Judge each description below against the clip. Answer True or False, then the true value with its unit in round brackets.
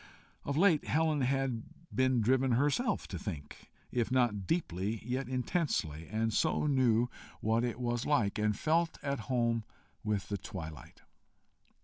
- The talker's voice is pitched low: True (120 Hz)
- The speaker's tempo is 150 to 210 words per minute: False (140 wpm)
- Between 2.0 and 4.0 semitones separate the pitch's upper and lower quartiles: False (4.4 semitones)